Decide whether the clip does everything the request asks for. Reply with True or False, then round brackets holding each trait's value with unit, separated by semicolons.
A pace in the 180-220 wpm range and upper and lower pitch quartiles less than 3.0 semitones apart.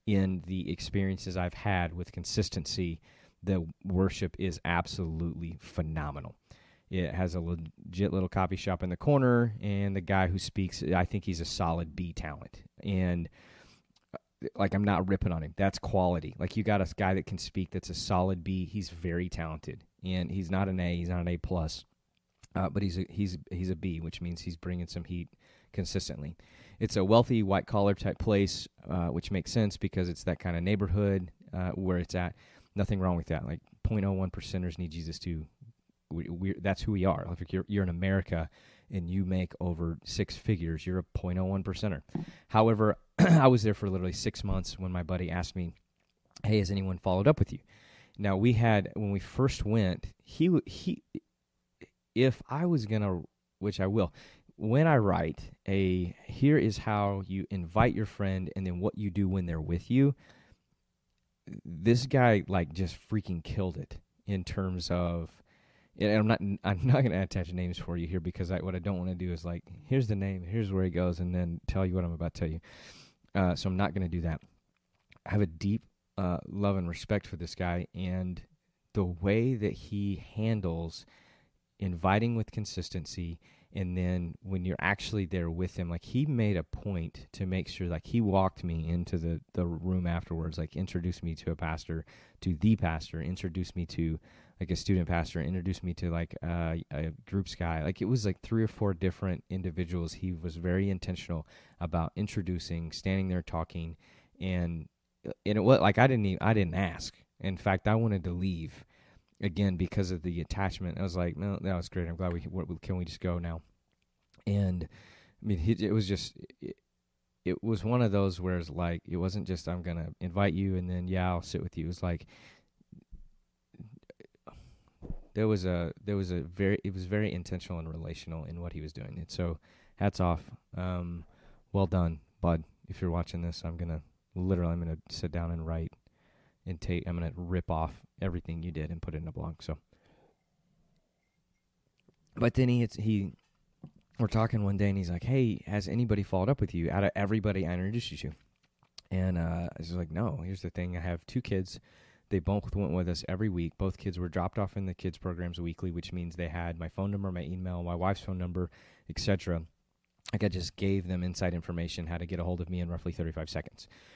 True (200 wpm; 2.5 semitones)